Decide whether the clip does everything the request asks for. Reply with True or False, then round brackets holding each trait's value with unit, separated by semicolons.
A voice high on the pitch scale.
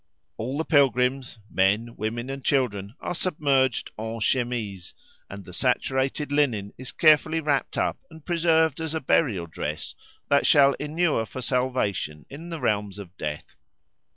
False (130 Hz)